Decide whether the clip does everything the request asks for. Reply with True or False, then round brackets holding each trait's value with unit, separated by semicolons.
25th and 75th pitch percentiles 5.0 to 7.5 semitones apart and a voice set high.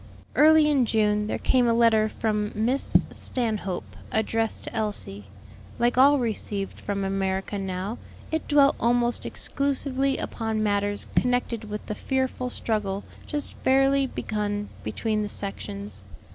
False (3.8 semitones; 220 Hz)